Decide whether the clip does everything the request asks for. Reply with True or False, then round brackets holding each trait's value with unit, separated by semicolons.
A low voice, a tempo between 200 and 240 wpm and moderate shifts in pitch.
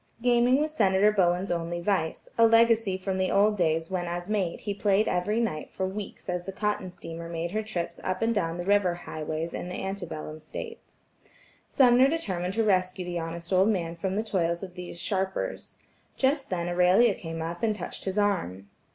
False (185 Hz; 205 wpm; 3.4 semitones)